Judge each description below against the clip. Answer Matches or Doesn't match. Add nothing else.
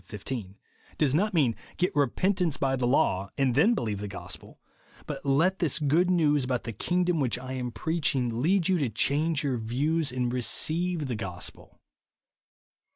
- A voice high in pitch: Doesn't match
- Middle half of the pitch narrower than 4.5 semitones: Doesn't match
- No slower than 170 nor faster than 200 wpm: Matches